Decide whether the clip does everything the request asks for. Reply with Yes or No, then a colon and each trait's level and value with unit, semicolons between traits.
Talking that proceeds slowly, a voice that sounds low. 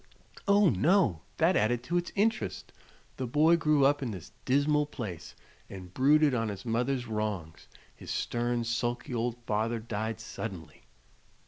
No: average, 145 wpm; low, 120 Hz